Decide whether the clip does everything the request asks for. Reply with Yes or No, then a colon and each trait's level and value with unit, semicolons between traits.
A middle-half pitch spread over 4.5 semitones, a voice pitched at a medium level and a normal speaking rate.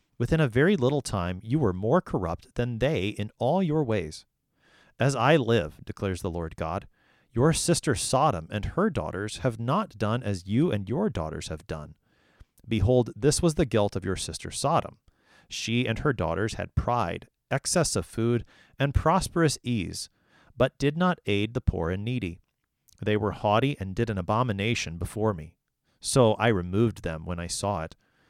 No: average, 5.3 semitones; low, 110 Hz; average, 180 wpm